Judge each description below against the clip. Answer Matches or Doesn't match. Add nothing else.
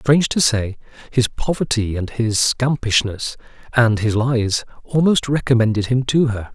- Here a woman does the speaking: Doesn't match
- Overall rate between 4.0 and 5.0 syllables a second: Matches